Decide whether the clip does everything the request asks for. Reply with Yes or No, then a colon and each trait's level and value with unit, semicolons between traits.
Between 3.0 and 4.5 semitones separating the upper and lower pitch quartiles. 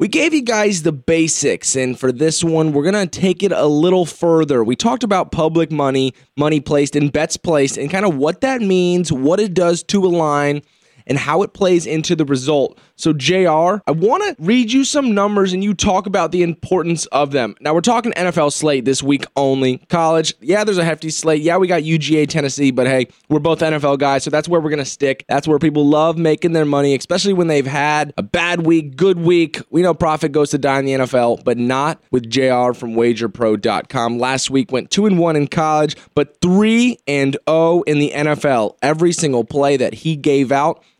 Yes: average, 3.9 semitones